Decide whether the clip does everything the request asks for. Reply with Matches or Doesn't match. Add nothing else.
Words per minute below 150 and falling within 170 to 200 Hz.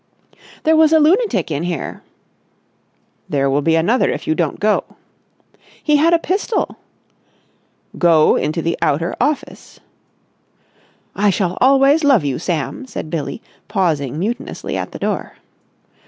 Matches